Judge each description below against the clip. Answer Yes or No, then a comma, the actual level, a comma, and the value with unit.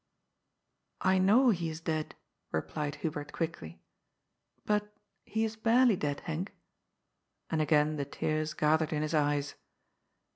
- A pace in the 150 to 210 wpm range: No, average, 140 wpm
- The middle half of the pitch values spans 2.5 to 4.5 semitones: Yes, average, 4.2 semitones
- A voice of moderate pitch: Yes, medium, 155 Hz